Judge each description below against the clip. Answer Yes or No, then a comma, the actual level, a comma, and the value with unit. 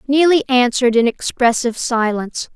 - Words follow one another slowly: Yes, slow, 120 wpm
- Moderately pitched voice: No, very high, 250 Hz